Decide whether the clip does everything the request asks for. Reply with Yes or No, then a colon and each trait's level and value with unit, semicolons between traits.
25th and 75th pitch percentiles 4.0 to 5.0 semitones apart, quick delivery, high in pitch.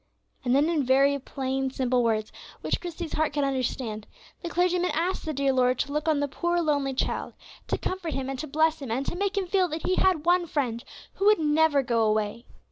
Yes: average, 4.6 semitones; fast, 220 wpm; very high, 285 Hz